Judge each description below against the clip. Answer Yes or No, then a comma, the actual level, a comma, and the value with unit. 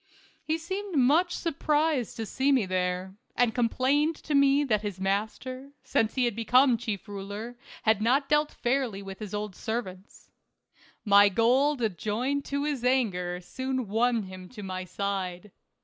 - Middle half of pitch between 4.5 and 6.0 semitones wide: Yes, wide, 5.5 semitones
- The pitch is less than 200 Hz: No, high, 230 Hz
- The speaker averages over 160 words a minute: No, average, 155 wpm